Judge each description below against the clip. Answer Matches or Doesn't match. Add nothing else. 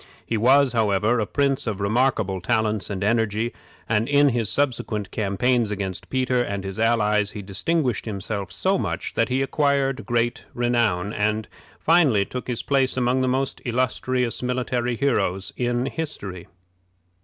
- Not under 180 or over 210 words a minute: Doesn't match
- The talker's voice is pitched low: Matches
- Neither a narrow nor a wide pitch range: Matches